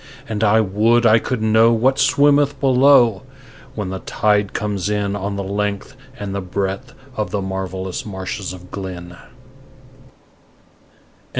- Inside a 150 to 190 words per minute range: No, slow, 135 wpm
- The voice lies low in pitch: Yes, low, 105 Hz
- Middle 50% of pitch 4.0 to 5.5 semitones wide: No, average, 3.3 semitones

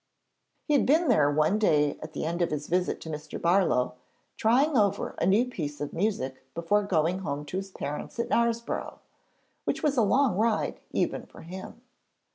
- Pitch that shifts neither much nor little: No, wide, 7.1 semitones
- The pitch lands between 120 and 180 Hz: No, high, 190 Hz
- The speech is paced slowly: No, average, 190 wpm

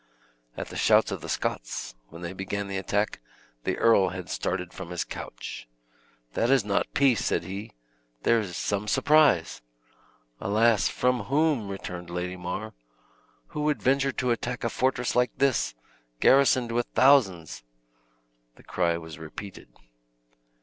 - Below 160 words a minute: Yes, average, 145 wpm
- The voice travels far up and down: Yes, wide, 5.7 semitones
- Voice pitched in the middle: No, low, 105 Hz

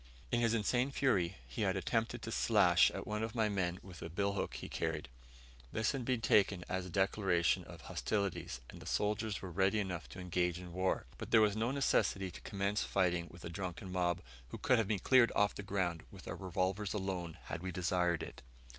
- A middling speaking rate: No, fast, 210 wpm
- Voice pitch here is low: Yes, very low, 95 Hz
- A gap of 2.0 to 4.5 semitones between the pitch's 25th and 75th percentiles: Yes, average, 3.2 semitones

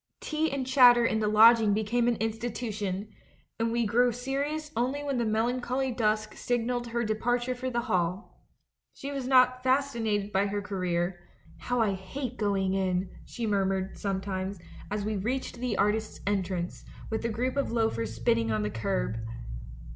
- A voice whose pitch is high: Yes, high, 220 Hz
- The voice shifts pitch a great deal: No, average, 4.0 semitones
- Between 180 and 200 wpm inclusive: No, average, 165 wpm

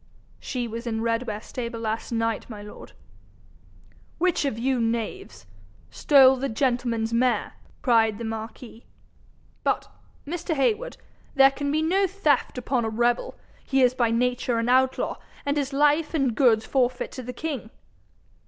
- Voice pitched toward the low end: No, very high, 250 Hz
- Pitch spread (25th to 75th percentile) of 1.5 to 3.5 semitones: Yes, average, 3.1 semitones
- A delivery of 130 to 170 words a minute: Yes, average, 150 wpm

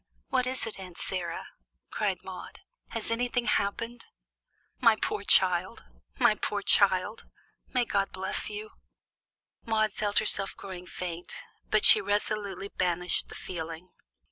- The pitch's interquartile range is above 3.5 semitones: No, average, 2.9 semitones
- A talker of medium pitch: No, high, 200 Hz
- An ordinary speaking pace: No, slow, 130 wpm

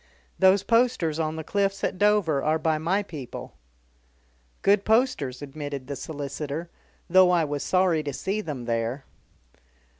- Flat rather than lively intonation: No, average, 5.2 semitones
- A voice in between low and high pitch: Yes, medium, 160 Hz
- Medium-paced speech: Yes, average, 145 wpm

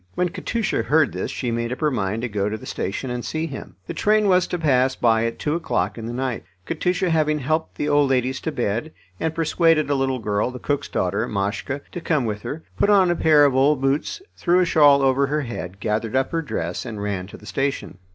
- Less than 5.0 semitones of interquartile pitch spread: No, wide, 5.6 semitones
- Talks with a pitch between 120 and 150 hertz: Yes, low, 135 Hz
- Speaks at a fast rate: Yes, fast, 240 wpm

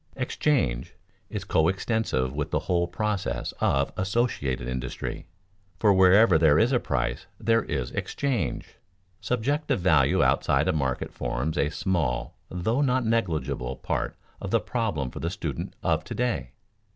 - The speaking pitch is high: No, very low, 85 Hz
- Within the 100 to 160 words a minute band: Yes, average, 140 wpm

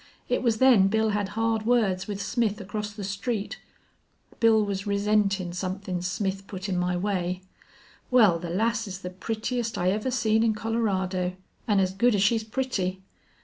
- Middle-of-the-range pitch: No, high, 205 Hz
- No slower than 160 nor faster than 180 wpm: Yes, average, 165 wpm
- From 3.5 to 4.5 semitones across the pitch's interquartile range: No, average, 2.9 semitones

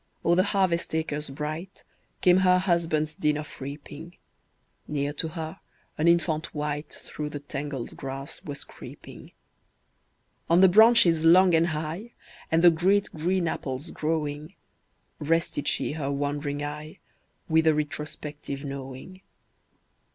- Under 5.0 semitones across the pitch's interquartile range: Yes, average, 2.7 semitones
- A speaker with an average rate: No, slow, 130 wpm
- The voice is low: No, medium, 155 Hz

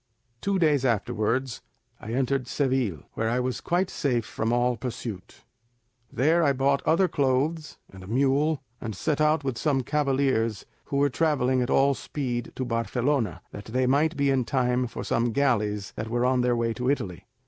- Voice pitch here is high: No, low, 130 Hz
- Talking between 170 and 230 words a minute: Yes, average, 180 wpm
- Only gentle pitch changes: No, average, 3.2 semitones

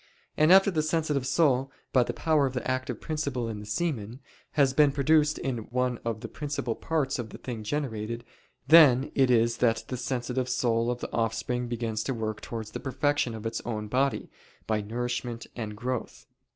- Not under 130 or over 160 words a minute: No, average, 190 wpm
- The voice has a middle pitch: No, low, 125 Hz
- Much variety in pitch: No, average, 3.4 semitones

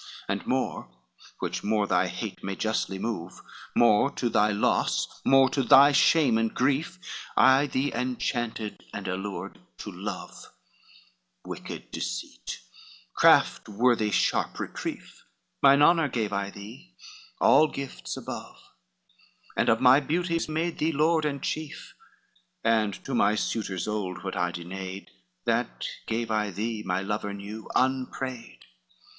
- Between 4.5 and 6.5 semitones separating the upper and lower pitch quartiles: Yes, average, 5.2 semitones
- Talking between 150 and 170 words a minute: No, slow, 135 wpm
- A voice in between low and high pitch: No, low, 115 Hz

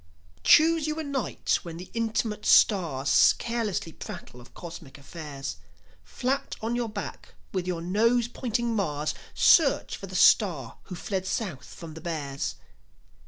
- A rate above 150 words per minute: No, average, 145 wpm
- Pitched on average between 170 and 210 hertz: Yes, high, 190 Hz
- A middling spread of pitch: No, wide, 6.5 semitones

